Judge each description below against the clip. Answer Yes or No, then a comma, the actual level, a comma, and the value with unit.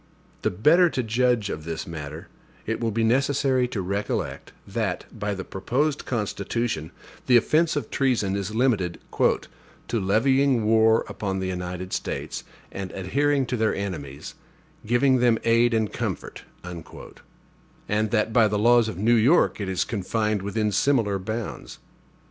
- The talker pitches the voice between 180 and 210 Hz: No, low, 110 Hz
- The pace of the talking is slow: No, average, 150 wpm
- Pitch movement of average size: Yes, average, 4.0 semitones